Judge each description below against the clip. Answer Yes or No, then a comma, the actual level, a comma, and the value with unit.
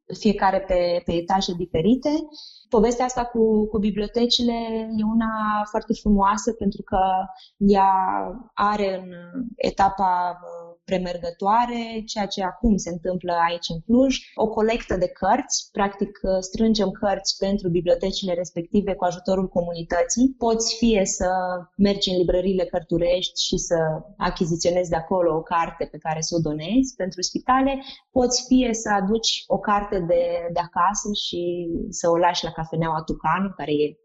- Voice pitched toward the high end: Yes, high, 195 Hz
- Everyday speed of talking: Yes, average, 145 wpm